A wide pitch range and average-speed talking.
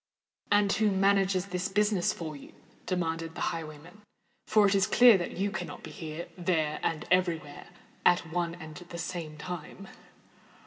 No: average, 3.3 semitones; average, 150 wpm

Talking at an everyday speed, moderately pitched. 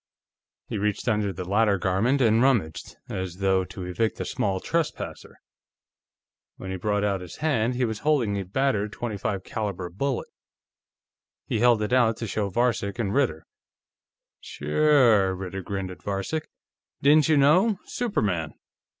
No: average, 150 wpm; low, 105 Hz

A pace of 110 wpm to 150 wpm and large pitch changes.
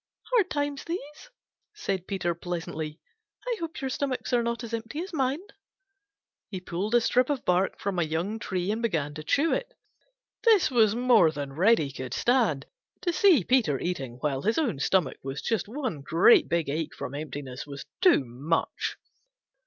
No: average, 175 wpm; wide, 9.0 semitones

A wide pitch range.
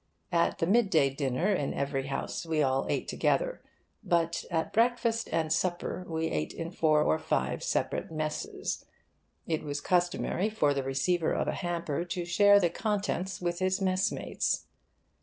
No: average, 3.7 semitones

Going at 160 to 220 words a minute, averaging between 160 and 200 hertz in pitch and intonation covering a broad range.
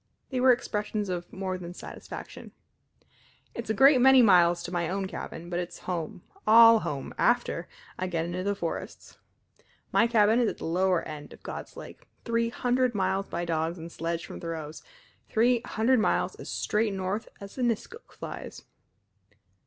No: average, 170 wpm; high, 190 Hz; average, 4.9 semitones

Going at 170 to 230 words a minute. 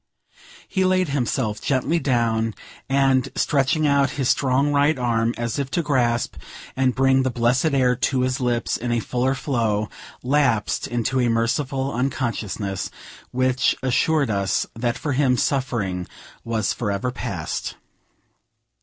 No: slow, 135 wpm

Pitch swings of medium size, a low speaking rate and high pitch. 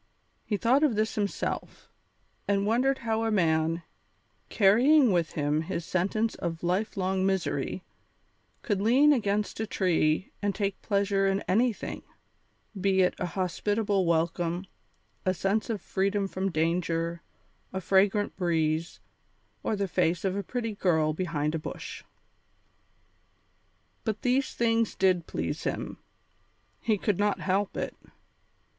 Yes: average, 3.7 semitones; slow, 130 wpm; high, 195 Hz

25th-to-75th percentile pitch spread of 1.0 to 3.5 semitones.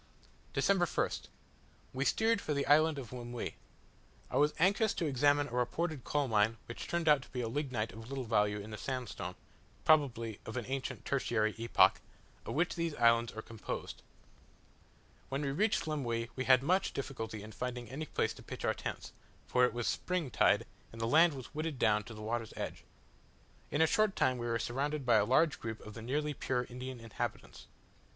No: average, 4.4 semitones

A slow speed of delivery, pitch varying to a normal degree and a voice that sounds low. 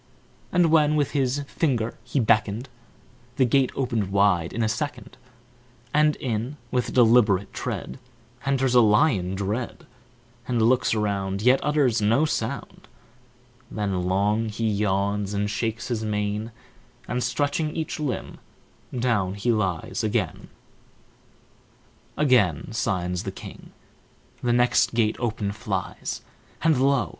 Yes: slow, 125 wpm; average, 4.0 semitones; low, 115 Hz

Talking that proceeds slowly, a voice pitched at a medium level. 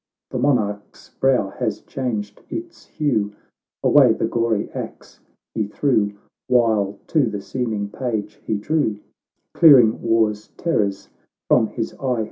No: slow, 125 wpm; low, 110 Hz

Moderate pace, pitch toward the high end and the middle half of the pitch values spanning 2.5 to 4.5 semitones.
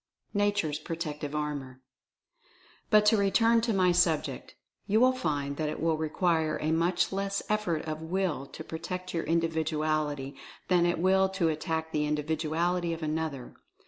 No: average, 150 wpm; medium, 160 Hz; average, 3.3 semitones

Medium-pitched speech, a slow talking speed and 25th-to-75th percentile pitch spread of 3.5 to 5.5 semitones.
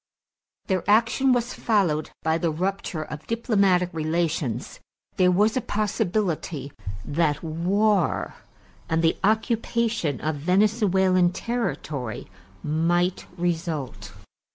Yes: medium, 180 Hz; slow, 100 wpm; average, 5.0 semitones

